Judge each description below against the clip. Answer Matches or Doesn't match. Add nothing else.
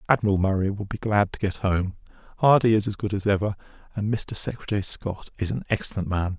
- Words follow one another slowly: Doesn't match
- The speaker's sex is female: Doesn't match